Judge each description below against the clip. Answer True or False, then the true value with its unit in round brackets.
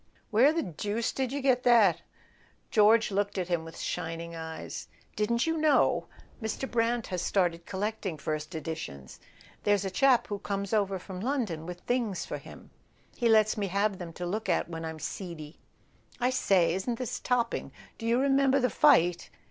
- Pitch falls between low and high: False (205 Hz)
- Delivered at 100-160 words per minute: False (180 wpm)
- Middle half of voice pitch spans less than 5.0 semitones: False (5.6 semitones)